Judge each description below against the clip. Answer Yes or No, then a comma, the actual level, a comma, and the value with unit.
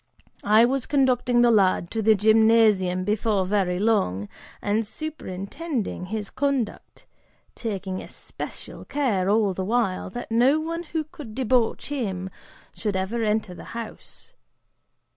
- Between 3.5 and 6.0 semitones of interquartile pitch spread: Yes, average, 4.3 semitones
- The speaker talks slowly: Yes, slow, 130 wpm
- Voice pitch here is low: No, high, 220 Hz